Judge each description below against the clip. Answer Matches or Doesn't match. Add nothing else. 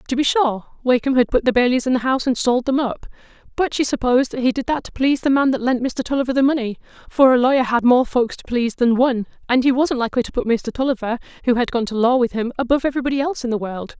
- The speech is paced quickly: Matches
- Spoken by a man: Doesn't match